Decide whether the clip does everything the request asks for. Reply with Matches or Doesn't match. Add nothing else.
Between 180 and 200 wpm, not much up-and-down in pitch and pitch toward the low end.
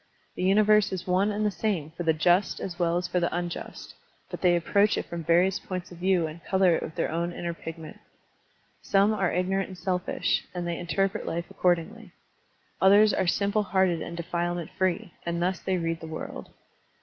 Doesn't match